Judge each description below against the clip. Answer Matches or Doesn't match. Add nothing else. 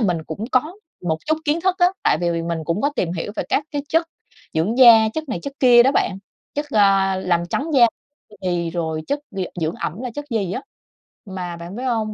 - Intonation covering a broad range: Matches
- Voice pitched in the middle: Doesn't match